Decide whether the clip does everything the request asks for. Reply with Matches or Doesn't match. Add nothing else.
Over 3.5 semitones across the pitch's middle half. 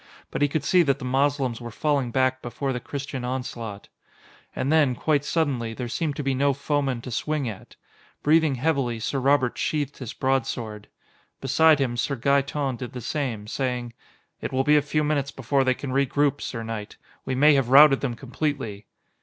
Doesn't match